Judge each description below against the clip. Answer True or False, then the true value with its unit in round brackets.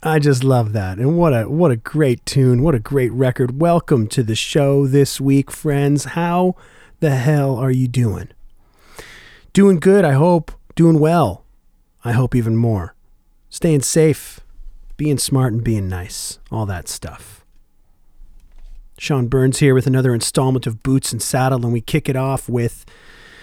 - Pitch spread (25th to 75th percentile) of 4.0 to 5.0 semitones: True (4.4 semitones)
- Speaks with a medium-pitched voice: False (130 Hz)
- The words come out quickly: False (165 wpm)